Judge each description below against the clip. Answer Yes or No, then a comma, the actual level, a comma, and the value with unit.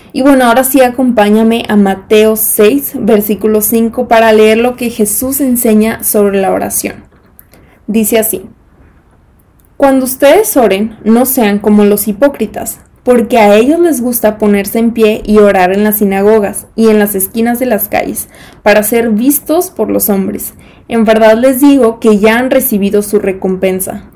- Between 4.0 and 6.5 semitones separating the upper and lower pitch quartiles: No, average, 2.8 semitones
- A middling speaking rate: Yes, average, 160 wpm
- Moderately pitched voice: No, high, 220 Hz